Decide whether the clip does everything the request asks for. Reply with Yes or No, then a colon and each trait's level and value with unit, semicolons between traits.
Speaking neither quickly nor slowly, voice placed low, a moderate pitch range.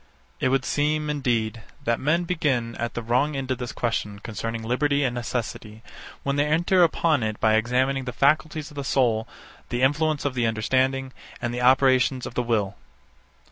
Yes: average, 185 wpm; low, 130 Hz; average, 3.5 semitones